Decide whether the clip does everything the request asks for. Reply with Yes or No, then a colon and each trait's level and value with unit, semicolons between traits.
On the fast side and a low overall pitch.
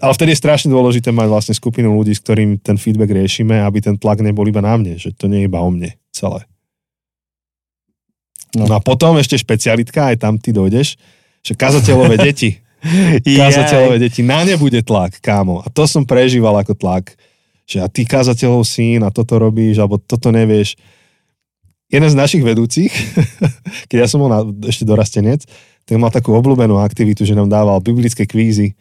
Yes: fast, 180 wpm; low, 115 Hz